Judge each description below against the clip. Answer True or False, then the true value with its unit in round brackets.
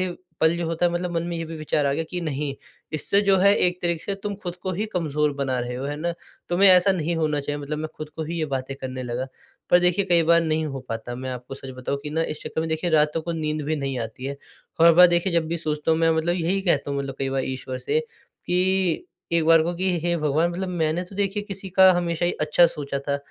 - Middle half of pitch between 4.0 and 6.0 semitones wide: False (3.5 semitones)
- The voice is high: False (160 Hz)